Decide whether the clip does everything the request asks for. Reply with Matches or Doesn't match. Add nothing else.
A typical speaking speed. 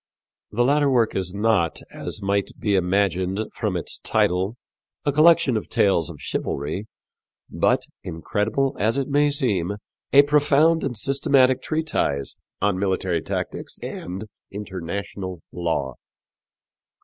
Doesn't match